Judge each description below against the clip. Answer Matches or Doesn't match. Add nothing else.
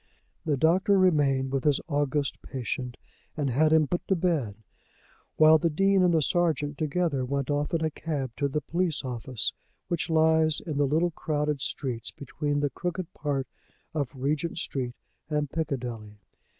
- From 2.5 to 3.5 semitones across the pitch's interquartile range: Matches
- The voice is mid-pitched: Matches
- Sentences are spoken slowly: Doesn't match